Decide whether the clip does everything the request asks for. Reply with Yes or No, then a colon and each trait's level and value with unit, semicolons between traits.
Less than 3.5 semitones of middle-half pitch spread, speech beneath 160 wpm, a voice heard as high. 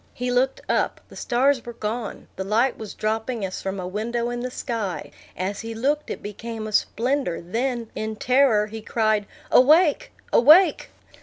No: average, 3.1 semitones; average, 170 wpm; high, 230 Hz